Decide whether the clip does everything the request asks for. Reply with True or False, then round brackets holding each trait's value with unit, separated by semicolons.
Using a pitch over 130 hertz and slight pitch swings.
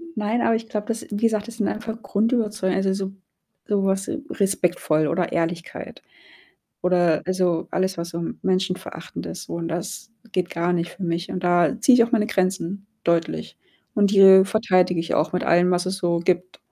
False (185 Hz; 3.1 semitones)